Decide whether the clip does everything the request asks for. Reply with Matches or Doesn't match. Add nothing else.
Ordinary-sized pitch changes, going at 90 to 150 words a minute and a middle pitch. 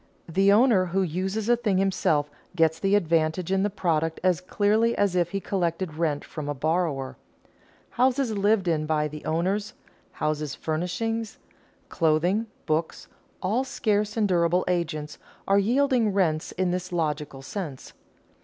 Matches